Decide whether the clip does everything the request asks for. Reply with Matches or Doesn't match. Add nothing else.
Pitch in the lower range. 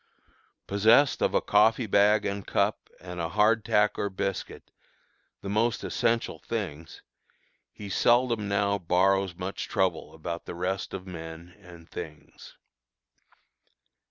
Matches